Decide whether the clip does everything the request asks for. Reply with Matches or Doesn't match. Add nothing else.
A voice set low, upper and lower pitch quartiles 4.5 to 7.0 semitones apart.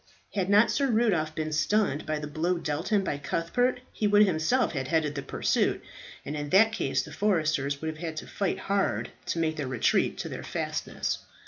Doesn't match